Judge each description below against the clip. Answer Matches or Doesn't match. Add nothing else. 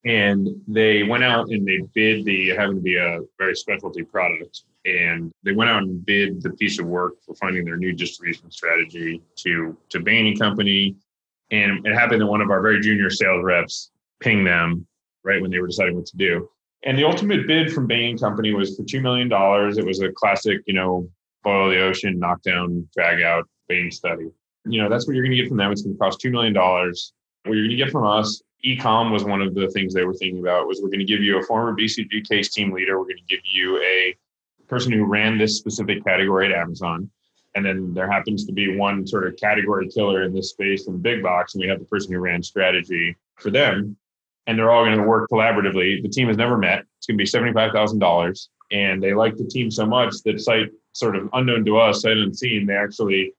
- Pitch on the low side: Matches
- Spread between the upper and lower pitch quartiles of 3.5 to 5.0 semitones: Doesn't match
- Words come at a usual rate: Doesn't match